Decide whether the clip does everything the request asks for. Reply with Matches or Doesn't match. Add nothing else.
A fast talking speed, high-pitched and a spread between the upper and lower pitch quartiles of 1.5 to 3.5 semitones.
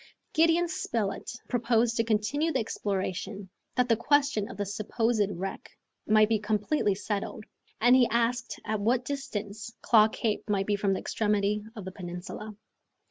Doesn't match